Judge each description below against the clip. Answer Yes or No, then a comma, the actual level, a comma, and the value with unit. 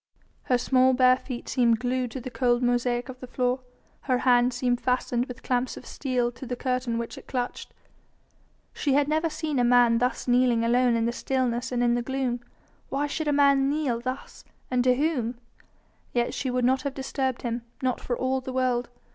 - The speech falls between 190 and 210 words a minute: Yes, average, 200 wpm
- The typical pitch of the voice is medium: No, very high, 250 Hz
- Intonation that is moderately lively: No, narrow, 1.4 semitones